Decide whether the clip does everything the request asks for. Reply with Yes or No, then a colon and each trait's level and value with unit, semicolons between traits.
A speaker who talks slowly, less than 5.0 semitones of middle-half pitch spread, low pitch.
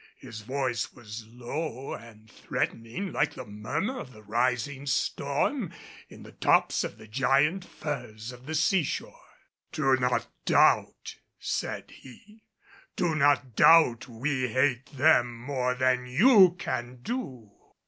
Yes: slow, 130 wpm; average, 3.9 semitones; low, 130 Hz